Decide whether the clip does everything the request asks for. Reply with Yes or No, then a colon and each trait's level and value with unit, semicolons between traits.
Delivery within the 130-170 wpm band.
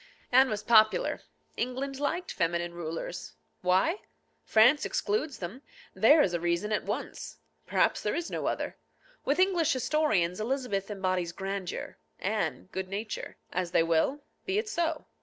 Yes: average, 145 wpm